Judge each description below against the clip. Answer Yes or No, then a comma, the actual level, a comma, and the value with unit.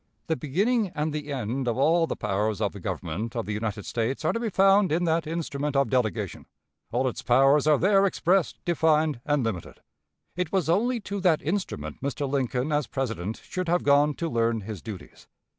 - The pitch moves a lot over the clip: Yes, wide, 6.6 semitones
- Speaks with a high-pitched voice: No, medium, 145 Hz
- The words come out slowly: No, average, 195 wpm